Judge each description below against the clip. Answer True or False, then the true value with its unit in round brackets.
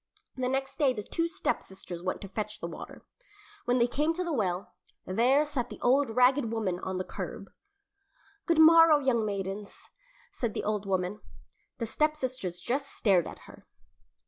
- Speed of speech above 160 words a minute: True (170 wpm)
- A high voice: True (240 Hz)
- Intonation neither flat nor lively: False (6.2 semitones)